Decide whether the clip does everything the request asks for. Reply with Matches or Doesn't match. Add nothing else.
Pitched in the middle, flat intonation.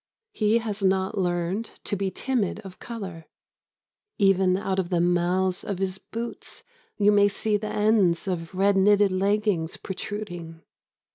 Doesn't match